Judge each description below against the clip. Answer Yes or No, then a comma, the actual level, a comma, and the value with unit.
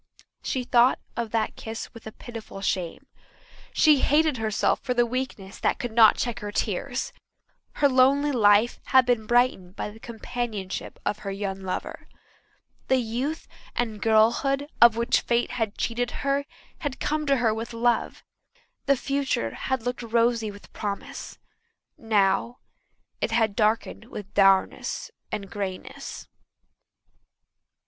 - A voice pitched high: Yes, high, 230 Hz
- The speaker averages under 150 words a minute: Yes, average, 140 wpm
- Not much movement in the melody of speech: No, average, 3.2 semitones